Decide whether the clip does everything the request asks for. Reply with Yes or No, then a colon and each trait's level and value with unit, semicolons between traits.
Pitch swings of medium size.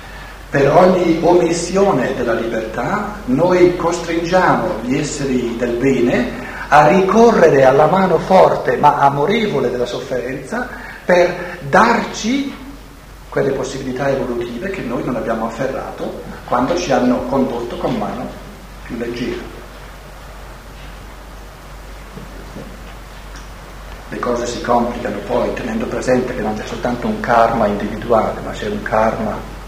No: wide, 7.1 semitones